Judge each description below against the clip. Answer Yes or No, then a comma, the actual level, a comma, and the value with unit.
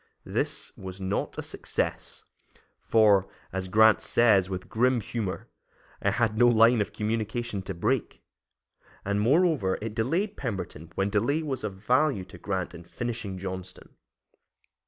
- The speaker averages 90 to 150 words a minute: Yes, average, 140 wpm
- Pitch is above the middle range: No, low, 105 Hz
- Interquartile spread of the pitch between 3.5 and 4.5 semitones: Yes, average, 4.0 semitones